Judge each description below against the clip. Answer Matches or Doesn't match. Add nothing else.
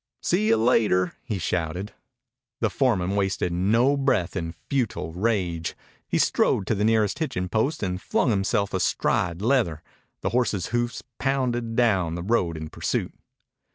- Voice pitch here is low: Matches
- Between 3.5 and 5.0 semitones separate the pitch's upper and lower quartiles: Matches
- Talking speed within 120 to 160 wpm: Matches